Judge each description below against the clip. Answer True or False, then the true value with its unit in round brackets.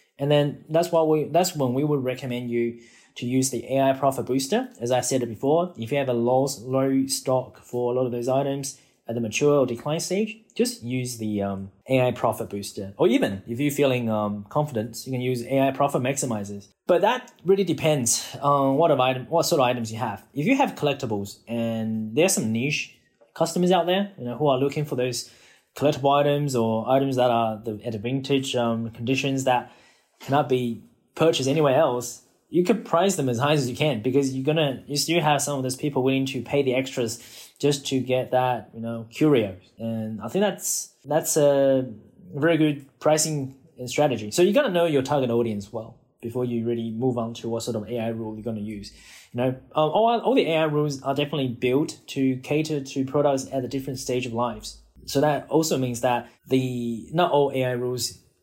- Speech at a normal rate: False (210 wpm)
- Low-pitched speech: True (130 Hz)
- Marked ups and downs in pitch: False (3.6 semitones)